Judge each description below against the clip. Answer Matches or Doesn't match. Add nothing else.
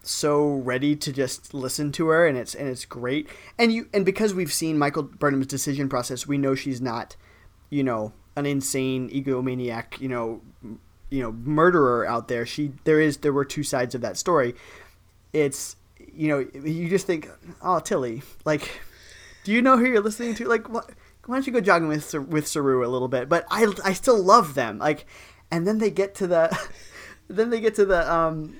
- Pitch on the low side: Doesn't match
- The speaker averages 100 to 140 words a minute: Doesn't match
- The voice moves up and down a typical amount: Doesn't match